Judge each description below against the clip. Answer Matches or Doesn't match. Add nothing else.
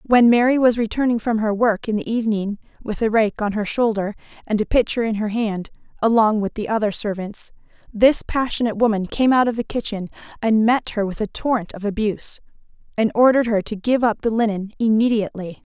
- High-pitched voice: Matches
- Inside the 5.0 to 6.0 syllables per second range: Matches